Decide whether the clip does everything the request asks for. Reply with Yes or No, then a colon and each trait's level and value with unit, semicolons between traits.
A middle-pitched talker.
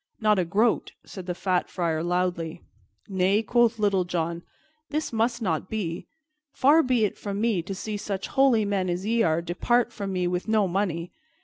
No: high, 195 Hz